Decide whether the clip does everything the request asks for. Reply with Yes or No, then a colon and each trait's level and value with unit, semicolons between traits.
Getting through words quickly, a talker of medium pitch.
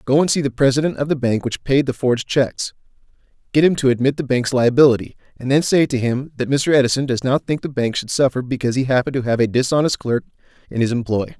No: fast, 240 wpm; low, 130 Hz